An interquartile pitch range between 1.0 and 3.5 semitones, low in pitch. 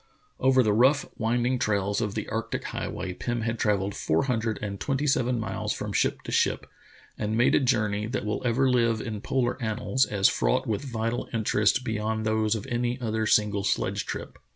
Yes: average, 2.7 semitones; low, 110 Hz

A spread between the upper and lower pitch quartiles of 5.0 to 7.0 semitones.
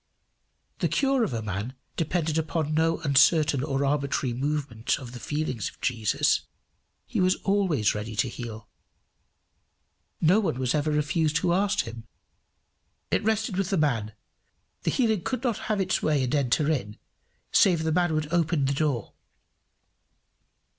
Yes: wide, 5.4 semitones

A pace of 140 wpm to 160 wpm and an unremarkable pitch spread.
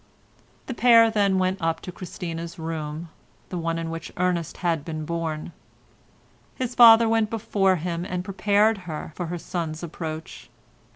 Yes: average, 155 wpm; average, 3.5 semitones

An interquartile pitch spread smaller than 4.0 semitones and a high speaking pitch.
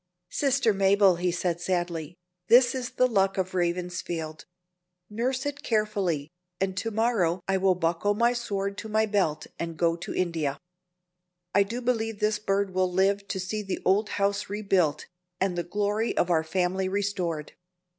Yes: average, 3.3 semitones; high, 195 Hz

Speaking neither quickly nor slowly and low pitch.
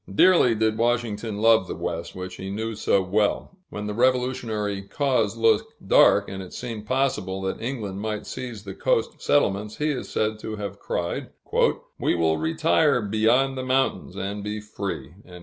Yes: average, 165 wpm; low, 110 Hz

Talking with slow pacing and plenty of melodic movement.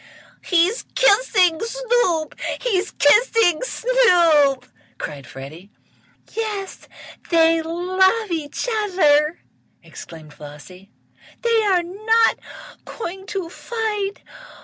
Yes: slow, 85 wpm; wide, 6.4 semitones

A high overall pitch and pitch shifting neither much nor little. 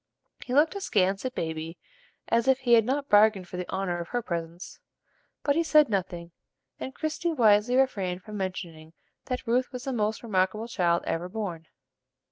No: high, 210 Hz; wide, 6.0 semitones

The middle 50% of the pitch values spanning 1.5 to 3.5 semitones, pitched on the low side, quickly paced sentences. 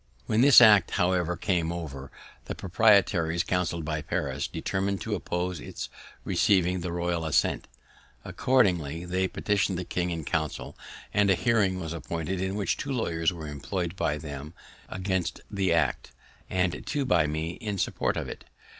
No: average, 2.8 semitones; very low, 90 Hz; average, 160 wpm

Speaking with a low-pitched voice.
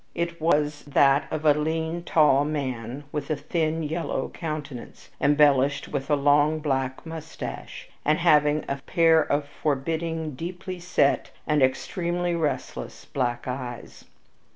No: medium, 150 Hz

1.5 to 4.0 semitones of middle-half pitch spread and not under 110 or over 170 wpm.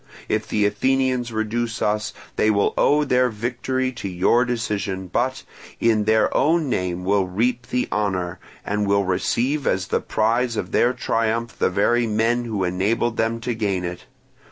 Yes: average, 3.4 semitones; average, 165 wpm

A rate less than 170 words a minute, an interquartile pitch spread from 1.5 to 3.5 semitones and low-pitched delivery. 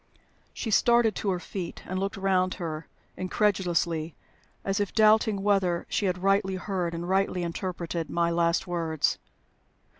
No: average, 145 wpm; narrow, 2.5 semitones; medium, 185 Hz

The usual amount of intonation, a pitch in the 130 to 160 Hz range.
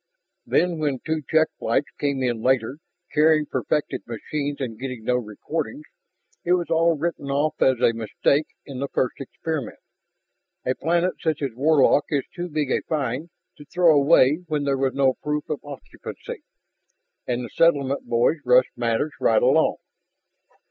Yes: average, 3.6 semitones; medium, 140 Hz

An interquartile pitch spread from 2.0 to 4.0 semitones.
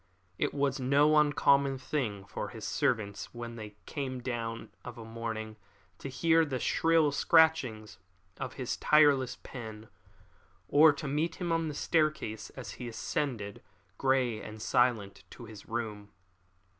No: average, 4.8 semitones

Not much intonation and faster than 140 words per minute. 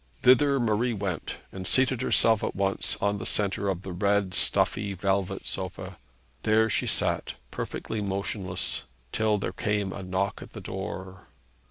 Yes: narrow, 2.2 semitones; average, 155 wpm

